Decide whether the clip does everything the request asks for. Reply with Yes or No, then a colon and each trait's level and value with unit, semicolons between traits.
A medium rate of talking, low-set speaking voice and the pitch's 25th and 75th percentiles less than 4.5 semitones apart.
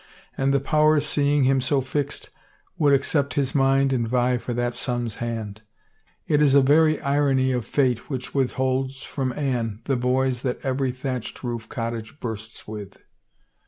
Yes: average, 160 wpm; low, 130 Hz; narrow, 2.4 semitones